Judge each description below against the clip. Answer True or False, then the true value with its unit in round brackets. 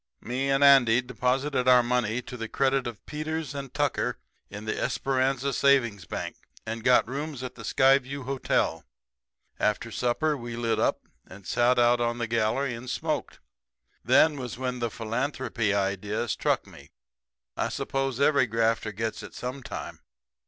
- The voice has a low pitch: True (125 Hz)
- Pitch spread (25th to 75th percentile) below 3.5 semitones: True (2.9 semitones)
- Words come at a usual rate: True (155 wpm)